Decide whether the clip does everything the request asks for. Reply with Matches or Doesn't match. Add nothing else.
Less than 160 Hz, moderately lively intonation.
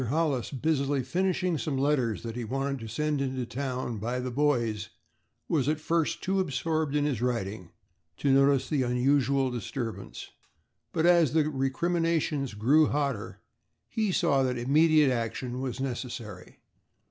Matches